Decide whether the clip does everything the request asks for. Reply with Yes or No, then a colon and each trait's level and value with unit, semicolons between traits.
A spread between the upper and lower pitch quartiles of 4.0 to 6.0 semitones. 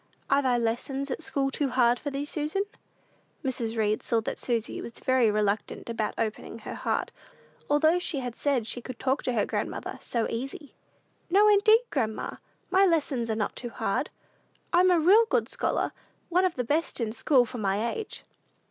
Yes: average, 5.2 semitones